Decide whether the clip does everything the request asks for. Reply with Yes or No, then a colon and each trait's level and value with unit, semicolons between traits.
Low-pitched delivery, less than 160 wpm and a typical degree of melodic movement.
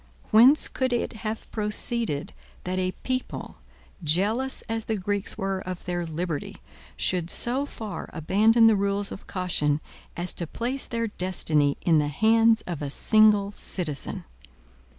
No: high, 200 Hz; average, 145 wpm; average, 4.4 semitones